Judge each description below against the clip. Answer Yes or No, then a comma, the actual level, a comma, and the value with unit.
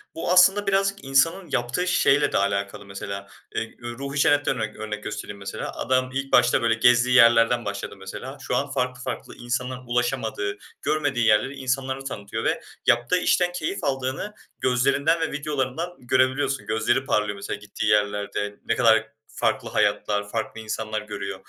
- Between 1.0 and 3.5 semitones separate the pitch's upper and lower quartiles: No, average, 4.4 semitones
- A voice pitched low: Yes, low, 125 Hz